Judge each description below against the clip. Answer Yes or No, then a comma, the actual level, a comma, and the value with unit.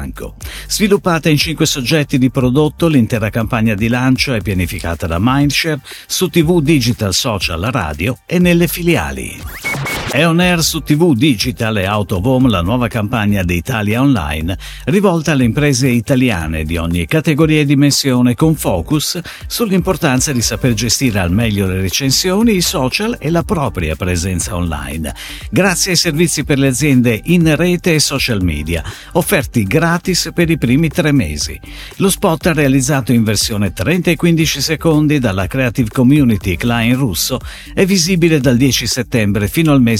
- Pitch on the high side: No, low, 135 Hz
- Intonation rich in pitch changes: Yes, wide, 6.9 semitones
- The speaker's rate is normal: Yes, average, 155 wpm